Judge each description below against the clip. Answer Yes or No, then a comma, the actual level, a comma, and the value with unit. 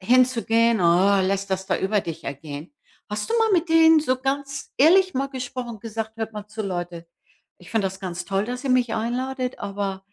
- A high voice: Yes, high, 225 Hz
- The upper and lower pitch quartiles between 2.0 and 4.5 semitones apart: No, average, 5.1 semitones